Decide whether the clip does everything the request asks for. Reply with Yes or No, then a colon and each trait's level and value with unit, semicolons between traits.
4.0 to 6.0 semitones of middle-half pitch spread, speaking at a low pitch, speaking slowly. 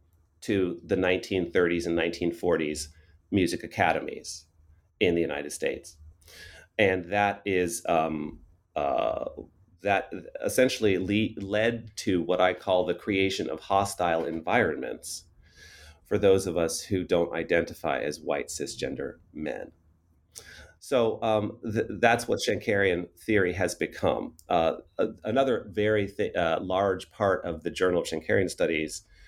No: average, 3.4 semitones; very low, 90 Hz; slow, 130 wpm